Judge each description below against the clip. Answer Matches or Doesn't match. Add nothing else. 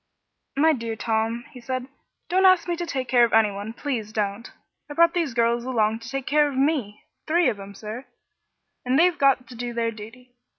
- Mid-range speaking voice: Doesn't match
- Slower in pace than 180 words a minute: Doesn't match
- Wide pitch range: Doesn't match